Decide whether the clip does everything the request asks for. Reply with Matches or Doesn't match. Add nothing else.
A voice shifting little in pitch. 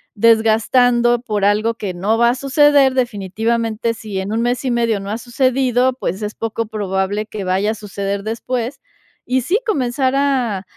Doesn't match